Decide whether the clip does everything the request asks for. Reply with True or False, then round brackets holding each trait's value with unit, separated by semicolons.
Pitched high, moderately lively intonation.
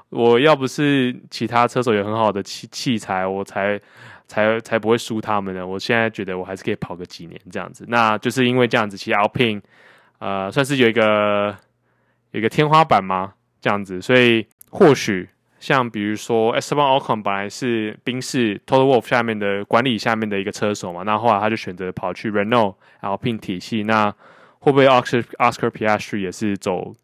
False (110 Hz; 3.1 semitones)